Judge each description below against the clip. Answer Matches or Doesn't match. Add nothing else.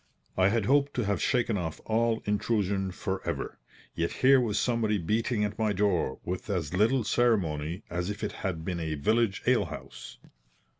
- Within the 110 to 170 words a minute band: Doesn't match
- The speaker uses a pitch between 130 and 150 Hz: Doesn't match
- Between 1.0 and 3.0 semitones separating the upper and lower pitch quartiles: Doesn't match